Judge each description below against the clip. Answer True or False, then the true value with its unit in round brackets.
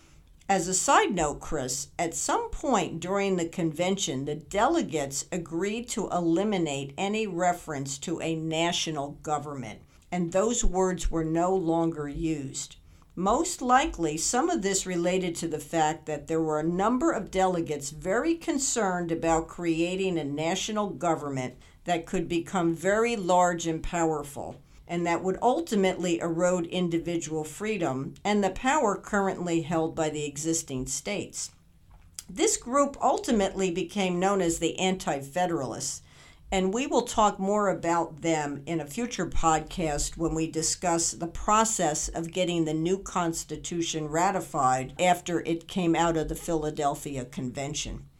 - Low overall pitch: False (170 Hz)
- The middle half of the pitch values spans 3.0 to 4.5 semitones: True (3.4 semitones)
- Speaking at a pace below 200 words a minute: True (140 wpm)